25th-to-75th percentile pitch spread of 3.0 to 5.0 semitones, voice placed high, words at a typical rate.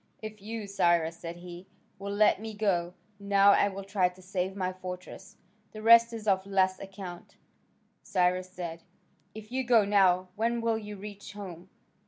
No: narrow, 2.5 semitones; high, 195 Hz; average, 170 wpm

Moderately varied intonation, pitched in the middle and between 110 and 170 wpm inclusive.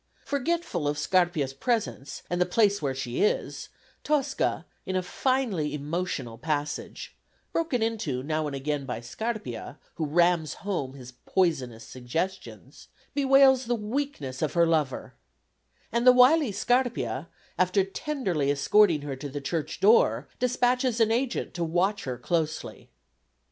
No: wide, 8.4 semitones; medium, 175 Hz; average, 140 wpm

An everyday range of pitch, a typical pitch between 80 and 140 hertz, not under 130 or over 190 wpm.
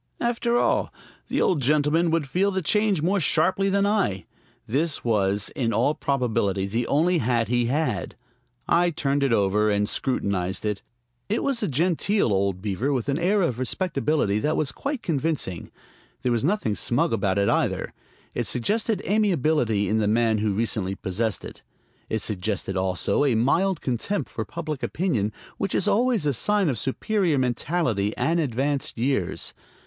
No: wide, 8.2 semitones; low, 135 Hz; average, 165 wpm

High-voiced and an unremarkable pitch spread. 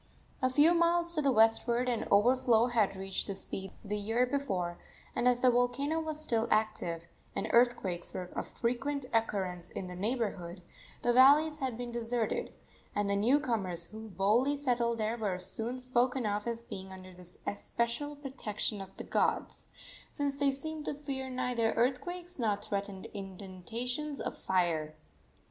Yes: high, 235 Hz; average, 4.8 semitones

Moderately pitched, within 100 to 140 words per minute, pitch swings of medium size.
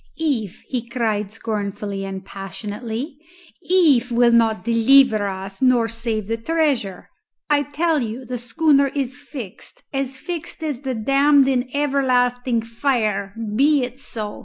No: high, 245 Hz; slow, 135 wpm; average, 4.2 semitones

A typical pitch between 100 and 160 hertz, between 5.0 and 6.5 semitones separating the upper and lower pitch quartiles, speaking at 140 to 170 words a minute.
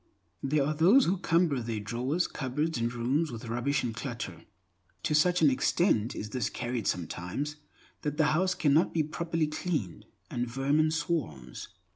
Yes: medium, 140 Hz; wide, 5.4 semitones; average, 160 wpm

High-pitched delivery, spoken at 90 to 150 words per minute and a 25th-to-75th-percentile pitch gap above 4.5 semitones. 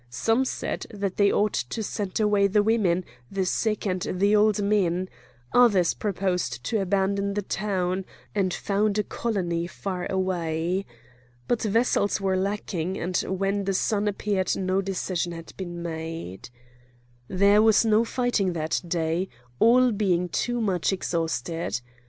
No: high, 195 Hz; average, 145 wpm; average, 2.8 semitones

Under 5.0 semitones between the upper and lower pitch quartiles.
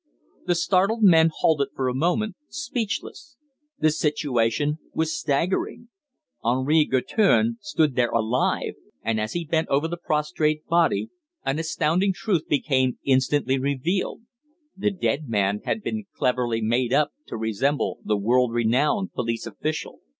No: wide, 5.5 semitones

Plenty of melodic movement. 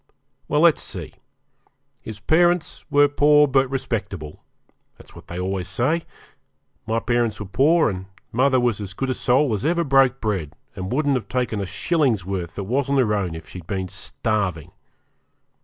Yes: wide, 6.4 semitones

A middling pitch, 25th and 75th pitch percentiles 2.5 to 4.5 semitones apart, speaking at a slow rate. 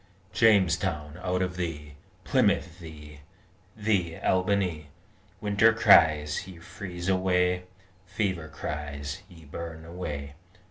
No: very low, 85 Hz; average, 3.6 semitones; slow, 100 wpm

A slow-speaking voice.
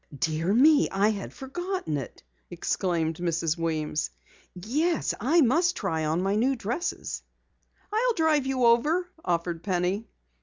Yes: slow, 130 wpm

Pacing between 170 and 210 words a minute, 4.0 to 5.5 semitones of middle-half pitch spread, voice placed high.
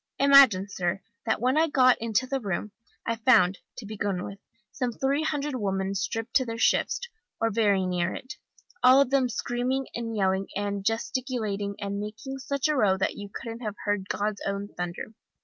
Yes: average, 185 wpm; average, 4.5 semitones; high, 220 Hz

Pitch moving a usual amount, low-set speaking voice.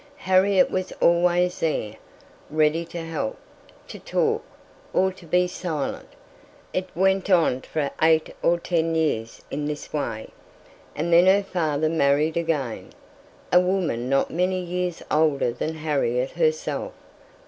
No: average, 3.3 semitones; medium, 165 Hz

